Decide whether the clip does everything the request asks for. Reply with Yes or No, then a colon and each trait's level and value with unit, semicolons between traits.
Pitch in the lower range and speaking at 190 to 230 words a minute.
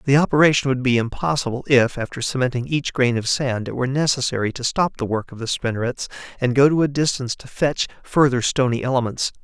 Yes: low, 130 Hz; fast, 205 wpm